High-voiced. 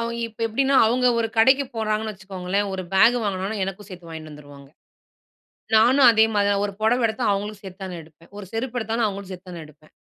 Yes: high, 205 Hz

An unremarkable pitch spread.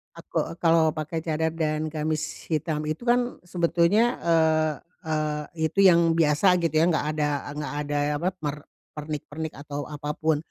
No: narrow, 1.7 semitones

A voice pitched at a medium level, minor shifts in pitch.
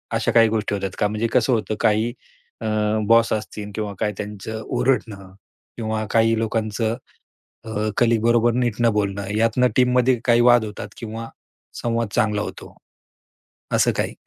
No: low, 110 Hz; narrow, 1.9 semitones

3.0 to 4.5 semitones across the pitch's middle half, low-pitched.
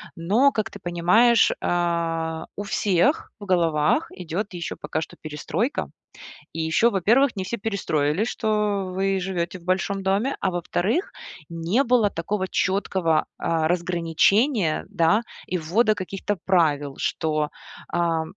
No: average, 4.0 semitones; medium, 185 Hz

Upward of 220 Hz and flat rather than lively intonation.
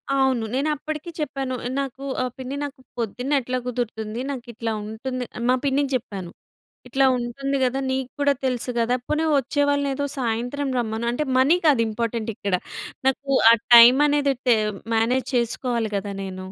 No: very high, 255 Hz; average, 3.0 semitones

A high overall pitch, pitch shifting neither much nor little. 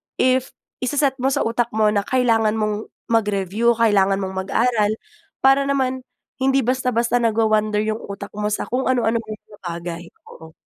Yes: high, 225 Hz; average, 3.4 semitones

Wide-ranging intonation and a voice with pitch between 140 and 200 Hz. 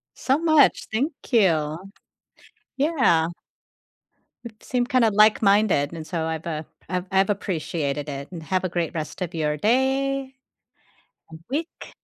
Yes: wide, 8.0 semitones; high, 190 Hz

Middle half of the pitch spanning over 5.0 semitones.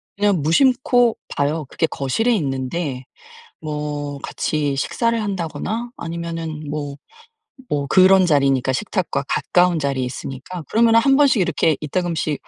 Yes: wide, 5.5 semitones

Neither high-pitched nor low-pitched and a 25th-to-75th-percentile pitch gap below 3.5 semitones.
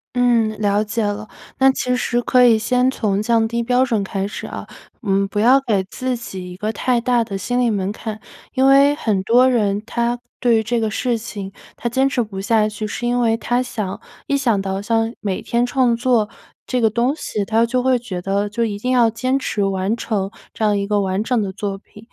No: high, 225 Hz; average, 3.1 semitones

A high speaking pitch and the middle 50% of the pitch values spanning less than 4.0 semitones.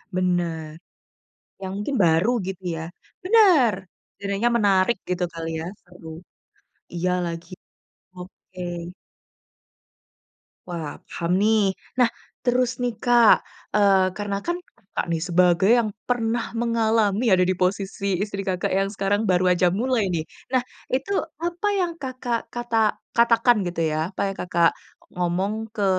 No: high, 200 Hz; average, 4.6 semitones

